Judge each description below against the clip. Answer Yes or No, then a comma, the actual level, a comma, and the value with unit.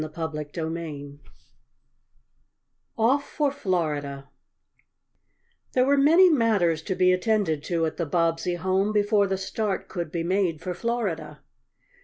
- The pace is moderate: No, slow, 125 wpm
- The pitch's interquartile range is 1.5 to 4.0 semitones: No, average, 4.9 semitones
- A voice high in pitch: No, medium, 180 Hz